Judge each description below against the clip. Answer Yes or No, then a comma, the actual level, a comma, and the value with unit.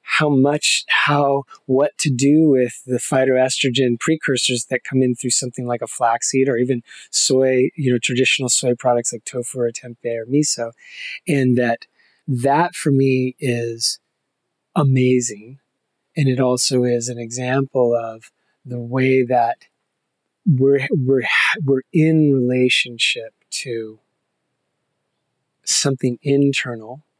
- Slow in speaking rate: Yes, slow, 125 wpm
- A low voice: Yes, low, 130 Hz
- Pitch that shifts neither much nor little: No, narrow, 2.2 semitones